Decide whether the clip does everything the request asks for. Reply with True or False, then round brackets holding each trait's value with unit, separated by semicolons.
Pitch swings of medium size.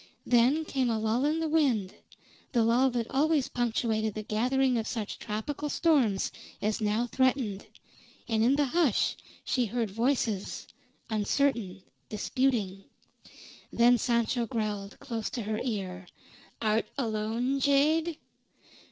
True (3.8 semitones)